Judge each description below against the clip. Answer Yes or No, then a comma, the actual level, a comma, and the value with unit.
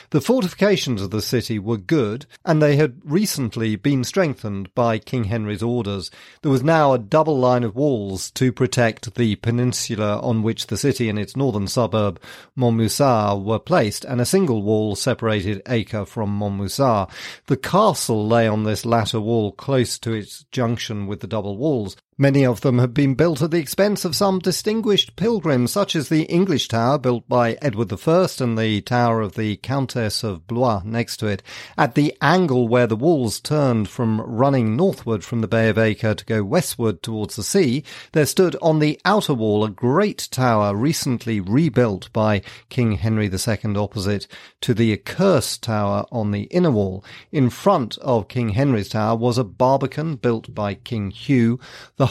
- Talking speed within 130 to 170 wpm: No, average, 180 wpm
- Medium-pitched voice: No, low, 120 Hz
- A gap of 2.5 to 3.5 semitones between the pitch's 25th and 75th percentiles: No, average, 4.5 semitones